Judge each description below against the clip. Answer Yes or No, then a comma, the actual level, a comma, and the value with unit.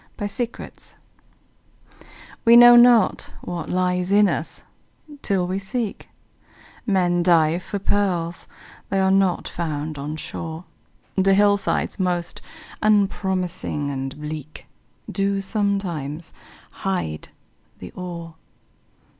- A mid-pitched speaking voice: Yes, medium, 180 Hz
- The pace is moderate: No, slow, 100 wpm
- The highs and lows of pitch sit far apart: No, average, 3.3 semitones